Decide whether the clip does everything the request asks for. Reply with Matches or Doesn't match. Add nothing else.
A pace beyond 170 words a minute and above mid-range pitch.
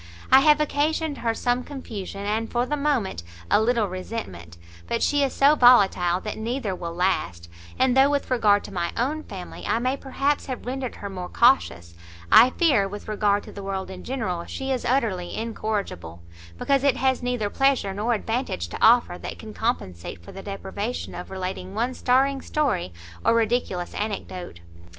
Matches